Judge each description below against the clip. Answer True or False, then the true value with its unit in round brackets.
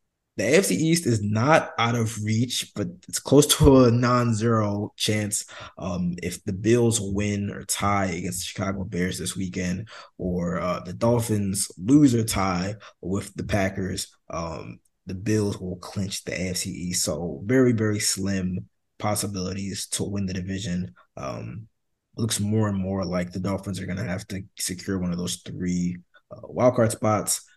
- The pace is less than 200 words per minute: True (170 wpm)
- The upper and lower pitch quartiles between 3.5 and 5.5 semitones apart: False (3.0 semitones)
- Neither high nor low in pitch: False (100 Hz)